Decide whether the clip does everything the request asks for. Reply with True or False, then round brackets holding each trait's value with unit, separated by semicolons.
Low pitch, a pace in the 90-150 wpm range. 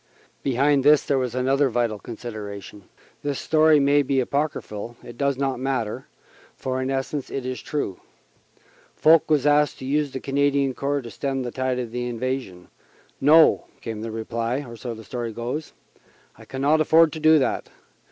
False (130 Hz; 165 wpm)